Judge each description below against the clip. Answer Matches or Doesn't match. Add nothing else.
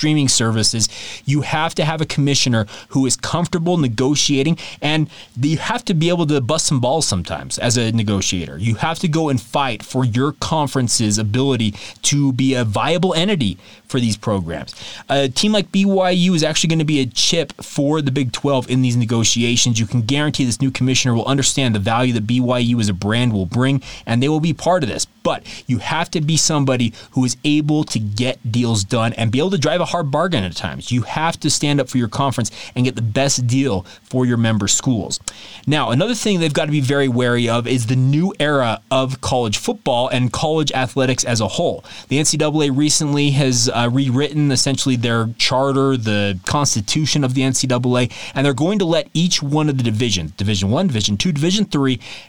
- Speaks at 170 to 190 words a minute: Doesn't match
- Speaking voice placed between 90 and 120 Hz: Doesn't match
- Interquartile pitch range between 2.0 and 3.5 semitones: Doesn't match